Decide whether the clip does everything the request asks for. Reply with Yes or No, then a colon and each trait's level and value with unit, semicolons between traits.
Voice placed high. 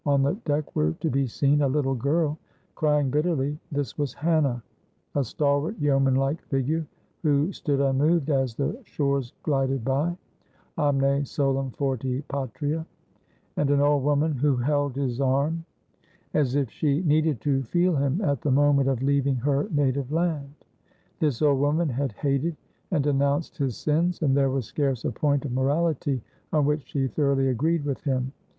No: medium, 140 Hz